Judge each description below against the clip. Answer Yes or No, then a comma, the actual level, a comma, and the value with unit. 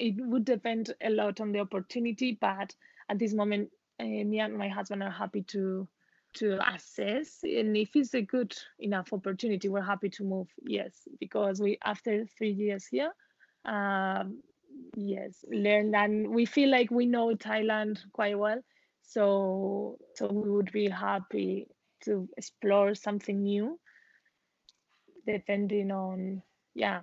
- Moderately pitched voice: No, high, 210 Hz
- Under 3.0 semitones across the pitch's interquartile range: Yes, narrow, 2.5 semitones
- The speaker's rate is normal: No, slow, 145 wpm